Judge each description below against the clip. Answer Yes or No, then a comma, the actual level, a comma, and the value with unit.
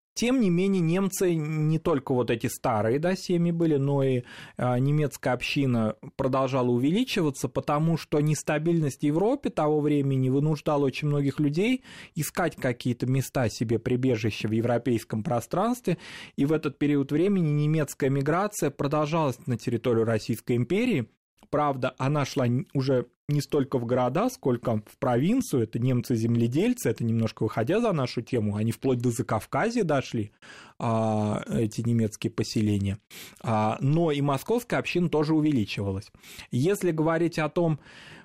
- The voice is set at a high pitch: No, medium, 140 Hz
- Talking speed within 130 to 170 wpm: Yes, average, 135 wpm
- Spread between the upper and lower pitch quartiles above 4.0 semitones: Yes, average, 4.6 semitones